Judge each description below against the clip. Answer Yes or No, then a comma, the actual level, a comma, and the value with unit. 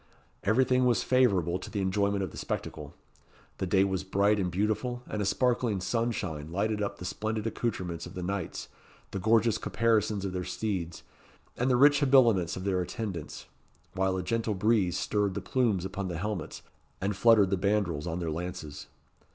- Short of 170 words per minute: No, average, 175 wpm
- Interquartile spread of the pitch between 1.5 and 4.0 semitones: Yes, average, 3.6 semitones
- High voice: No, low, 100 Hz